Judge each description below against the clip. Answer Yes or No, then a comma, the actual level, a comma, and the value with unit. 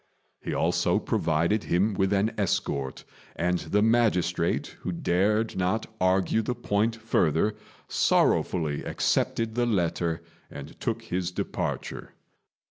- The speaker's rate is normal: No, slow, 120 wpm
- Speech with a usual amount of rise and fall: Yes, average, 4.2 semitones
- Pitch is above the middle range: No, very low, 95 Hz